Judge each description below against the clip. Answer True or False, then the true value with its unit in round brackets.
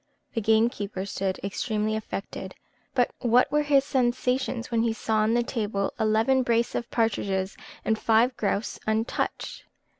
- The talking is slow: False (145 wpm)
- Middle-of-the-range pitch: False (225 Hz)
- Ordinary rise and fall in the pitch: False (2.3 semitones)